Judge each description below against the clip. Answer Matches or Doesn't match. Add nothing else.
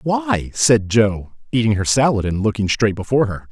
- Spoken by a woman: Doesn't match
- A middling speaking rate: Matches